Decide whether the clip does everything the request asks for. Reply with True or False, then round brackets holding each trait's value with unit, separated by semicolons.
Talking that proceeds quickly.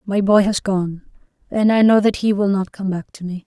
True (260 wpm)